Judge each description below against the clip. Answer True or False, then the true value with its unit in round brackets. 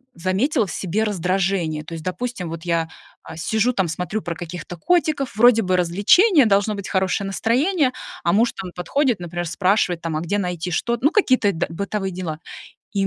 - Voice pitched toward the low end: False (190 Hz)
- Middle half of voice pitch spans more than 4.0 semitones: True (4.5 semitones)